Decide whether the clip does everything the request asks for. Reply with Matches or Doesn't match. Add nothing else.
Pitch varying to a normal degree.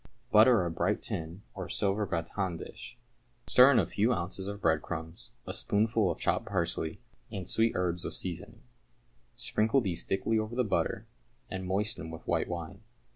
Matches